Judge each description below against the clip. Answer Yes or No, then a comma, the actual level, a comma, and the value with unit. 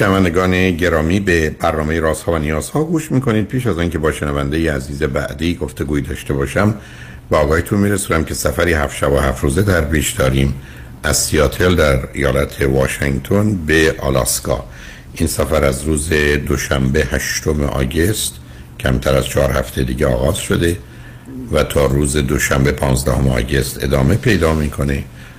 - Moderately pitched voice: No, very low, 75 Hz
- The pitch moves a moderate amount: Yes, average, 3.9 semitones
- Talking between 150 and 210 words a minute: Yes, fast, 155 wpm